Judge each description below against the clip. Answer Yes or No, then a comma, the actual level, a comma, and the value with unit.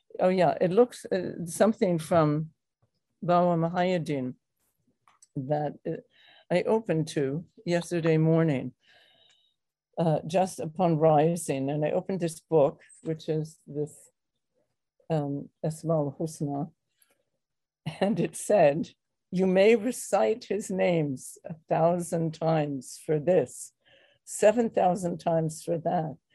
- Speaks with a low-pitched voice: No, medium, 165 Hz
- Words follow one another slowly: Yes, slow, 110 wpm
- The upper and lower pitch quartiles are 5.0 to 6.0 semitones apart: No, average, 2.9 semitones